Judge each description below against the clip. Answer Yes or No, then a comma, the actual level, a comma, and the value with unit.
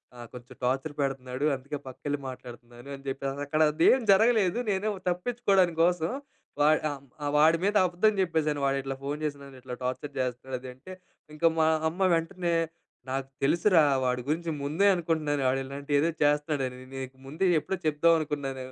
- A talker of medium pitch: Yes, medium, 145 Hz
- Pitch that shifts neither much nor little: Yes, average, 4.0 semitones